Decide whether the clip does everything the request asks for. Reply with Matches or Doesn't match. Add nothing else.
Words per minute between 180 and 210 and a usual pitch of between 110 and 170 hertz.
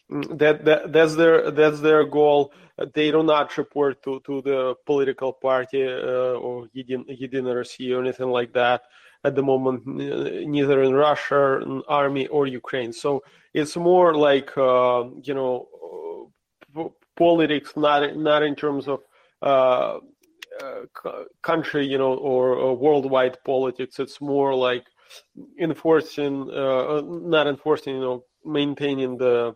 Doesn't match